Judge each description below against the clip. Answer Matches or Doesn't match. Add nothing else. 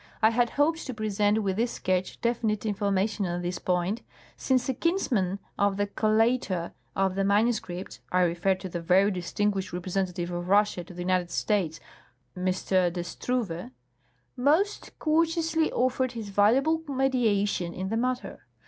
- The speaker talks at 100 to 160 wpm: Matches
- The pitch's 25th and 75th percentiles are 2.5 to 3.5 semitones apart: Doesn't match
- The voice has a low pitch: Doesn't match